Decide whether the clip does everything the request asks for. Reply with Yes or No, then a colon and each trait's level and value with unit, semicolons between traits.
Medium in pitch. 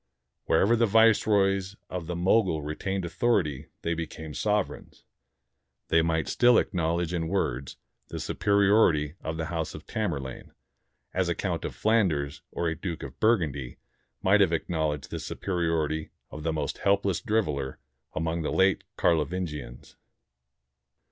No: very low, 85 Hz